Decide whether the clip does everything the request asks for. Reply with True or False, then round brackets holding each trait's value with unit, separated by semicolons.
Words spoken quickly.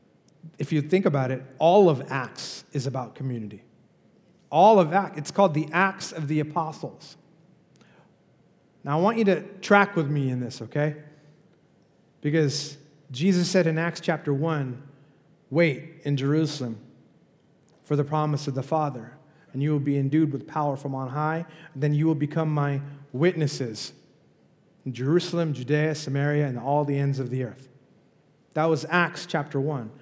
False (160 wpm)